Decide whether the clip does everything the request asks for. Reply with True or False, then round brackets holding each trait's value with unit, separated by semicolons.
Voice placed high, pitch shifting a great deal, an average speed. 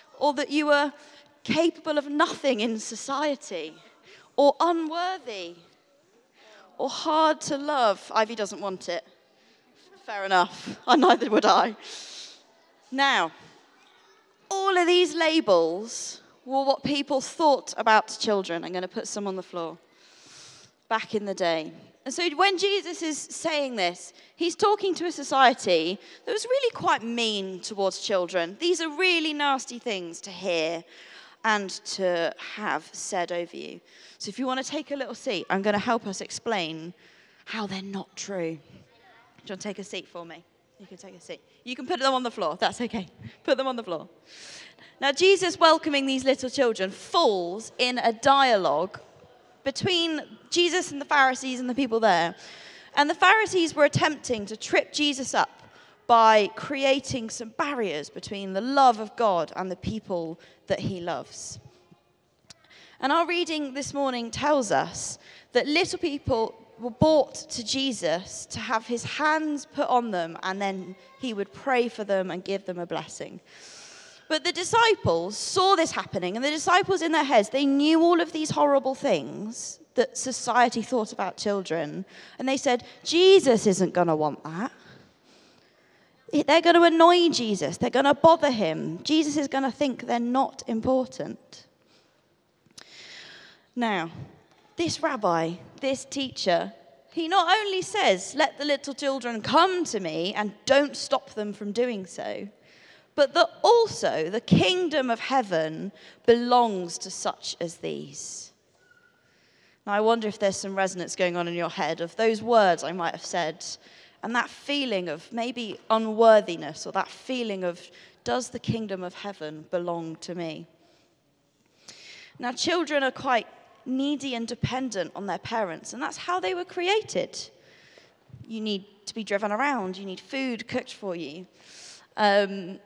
True (245 Hz; 7.2 semitones; 160 wpm)